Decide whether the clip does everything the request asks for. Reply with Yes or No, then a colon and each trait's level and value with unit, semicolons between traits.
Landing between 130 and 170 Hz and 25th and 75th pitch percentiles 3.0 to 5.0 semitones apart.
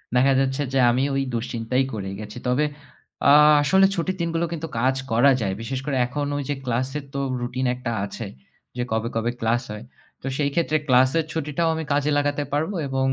Yes: low, 135 Hz; average, 3.4 semitones